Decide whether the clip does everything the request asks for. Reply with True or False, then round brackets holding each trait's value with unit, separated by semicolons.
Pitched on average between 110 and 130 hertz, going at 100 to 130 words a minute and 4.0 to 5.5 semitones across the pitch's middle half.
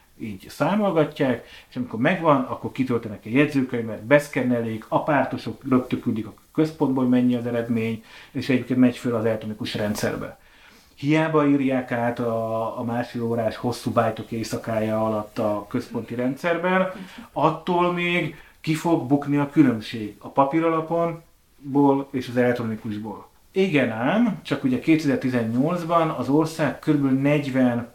True (125 Hz; 125 wpm; 4.7 semitones)